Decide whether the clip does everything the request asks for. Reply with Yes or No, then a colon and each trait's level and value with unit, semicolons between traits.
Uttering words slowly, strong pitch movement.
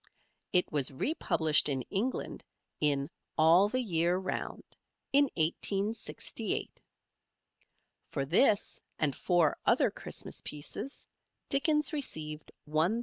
Yes: slow, 100 wpm; wide, 6.5 semitones